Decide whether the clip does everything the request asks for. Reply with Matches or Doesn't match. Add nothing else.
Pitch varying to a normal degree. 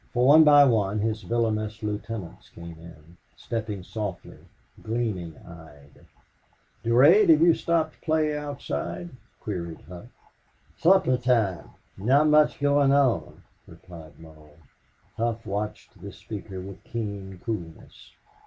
Doesn't match